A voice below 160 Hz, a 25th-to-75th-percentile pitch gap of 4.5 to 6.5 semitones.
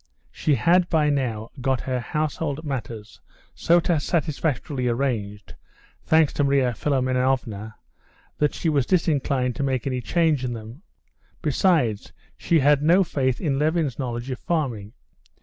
No: low, 135 Hz; average, 4.0 semitones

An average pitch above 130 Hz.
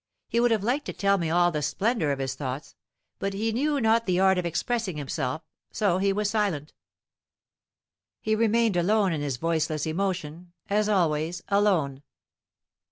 Yes: medium, 185 Hz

